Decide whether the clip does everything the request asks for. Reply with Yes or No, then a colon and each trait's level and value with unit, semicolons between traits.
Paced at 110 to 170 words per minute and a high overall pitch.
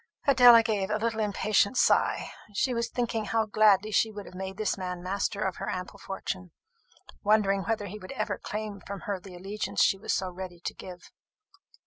No: average, 190 wpm; high, 205 Hz